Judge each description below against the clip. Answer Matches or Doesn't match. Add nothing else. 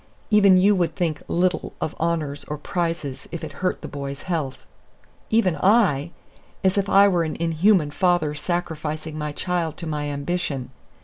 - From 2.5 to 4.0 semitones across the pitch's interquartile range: Matches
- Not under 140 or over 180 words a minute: Matches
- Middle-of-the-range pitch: Matches